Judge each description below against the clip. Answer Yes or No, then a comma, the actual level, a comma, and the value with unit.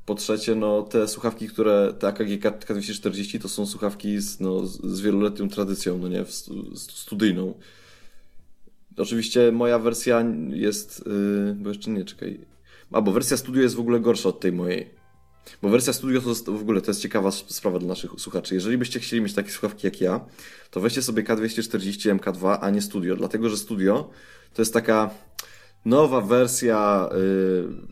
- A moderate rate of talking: No, fast, 170 wpm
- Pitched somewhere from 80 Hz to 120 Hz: Yes, low, 105 Hz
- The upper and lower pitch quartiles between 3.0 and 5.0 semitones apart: No, narrow, 2.6 semitones